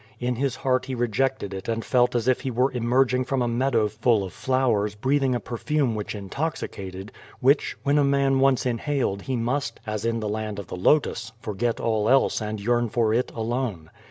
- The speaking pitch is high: No, low, 120 Hz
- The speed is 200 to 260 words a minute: Yes, fast, 205 wpm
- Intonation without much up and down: No, average, 3.5 semitones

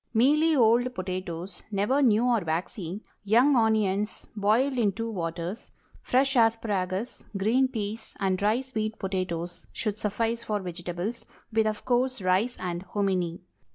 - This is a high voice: Yes, high, 210 Hz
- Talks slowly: Yes, slow, 125 wpm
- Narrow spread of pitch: No, average, 4.0 semitones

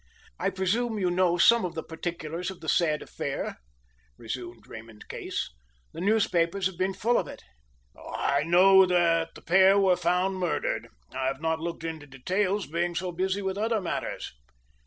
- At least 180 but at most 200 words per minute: No, average, 170 wpm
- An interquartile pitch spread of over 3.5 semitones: No, average, 2.7 semitones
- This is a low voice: No, medium, 175 Hz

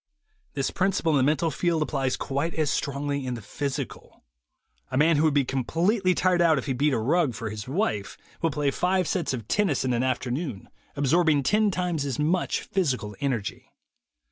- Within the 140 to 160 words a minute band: No, average, 195 wpm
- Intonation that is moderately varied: Yes, average, 4.6 semitones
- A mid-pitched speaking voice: Yes, medium, 145 Hz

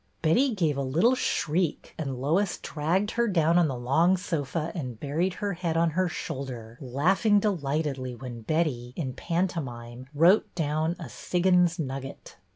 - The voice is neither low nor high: Yes, medium, 160 Hz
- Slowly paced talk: No, average, 155 wpm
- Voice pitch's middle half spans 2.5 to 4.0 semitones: No, average, 4.9 semitones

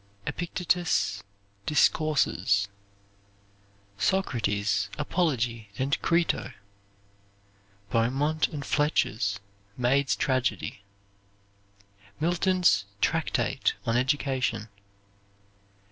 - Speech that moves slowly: Yes, slow, 55 wpm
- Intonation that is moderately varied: No, wide, 6.0 semitones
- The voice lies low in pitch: Yes, low, 130 Hz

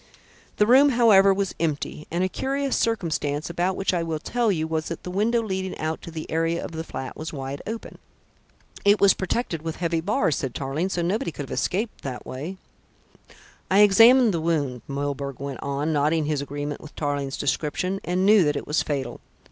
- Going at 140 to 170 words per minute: No, average, 195 wpm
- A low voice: No, medium, 165 Hz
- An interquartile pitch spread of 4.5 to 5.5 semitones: Yes, average, 5.0 semitones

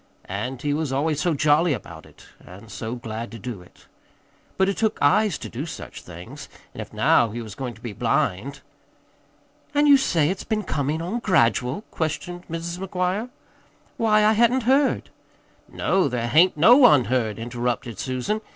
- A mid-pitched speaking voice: Yes, medium, 150 Hz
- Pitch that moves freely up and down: Yes, wide, 8.3 semitones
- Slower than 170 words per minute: No, average, 180 wpm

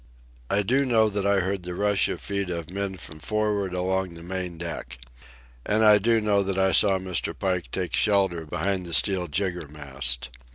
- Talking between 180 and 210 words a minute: Yes, average, 190 wpm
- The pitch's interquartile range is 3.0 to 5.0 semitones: No, narrow, 2.5 semitones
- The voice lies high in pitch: No, very low, 95 Hz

